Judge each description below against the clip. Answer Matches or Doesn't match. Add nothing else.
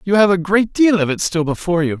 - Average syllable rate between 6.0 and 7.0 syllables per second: Matches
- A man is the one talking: Matches